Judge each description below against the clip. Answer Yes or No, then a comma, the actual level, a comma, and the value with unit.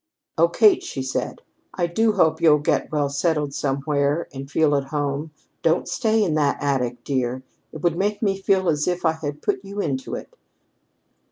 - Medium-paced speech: Yes, average, 185 wpm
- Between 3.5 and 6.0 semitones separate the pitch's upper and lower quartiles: Yes, average, 4.0 semitones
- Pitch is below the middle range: No, medium, 155 Hz